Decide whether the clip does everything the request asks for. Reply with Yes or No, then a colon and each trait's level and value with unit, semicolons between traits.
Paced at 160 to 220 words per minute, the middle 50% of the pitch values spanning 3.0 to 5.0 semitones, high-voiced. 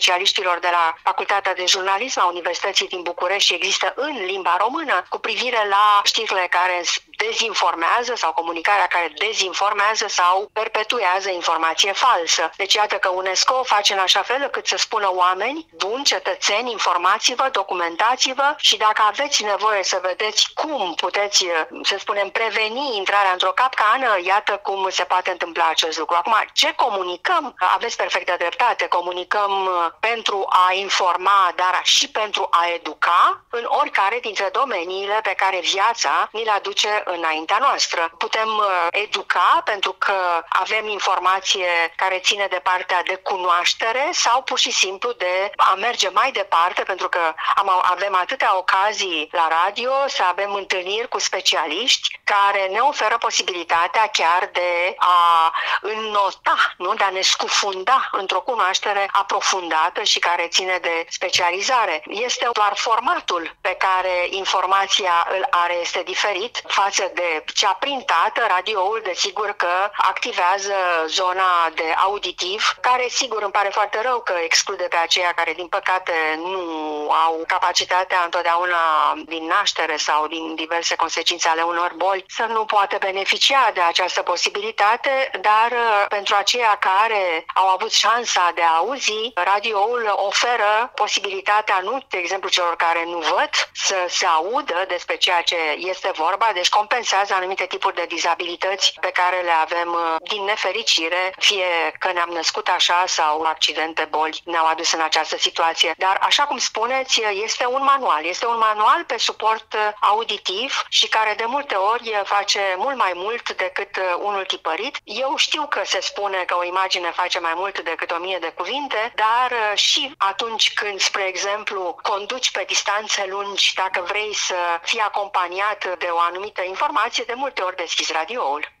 No: average, 150 wpm; average, 3.3 semitones; high, 195 Hz